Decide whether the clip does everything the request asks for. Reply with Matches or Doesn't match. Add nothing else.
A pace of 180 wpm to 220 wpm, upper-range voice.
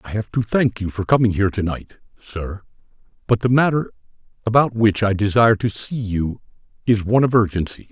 Doesn't match